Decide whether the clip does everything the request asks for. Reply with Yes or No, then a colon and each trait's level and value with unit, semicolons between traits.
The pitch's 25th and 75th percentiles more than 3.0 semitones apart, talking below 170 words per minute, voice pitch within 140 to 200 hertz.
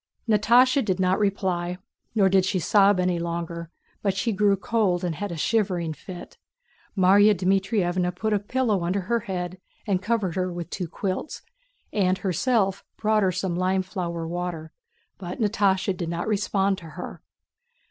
No: narrow, 2.6 semitones; average, 160 wpm; high, 190 Hz